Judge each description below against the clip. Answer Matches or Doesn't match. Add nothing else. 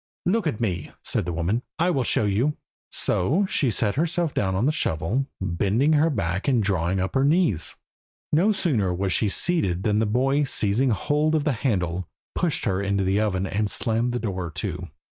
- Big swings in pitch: Matches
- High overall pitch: Doesn't match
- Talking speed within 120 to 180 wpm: Doesn't match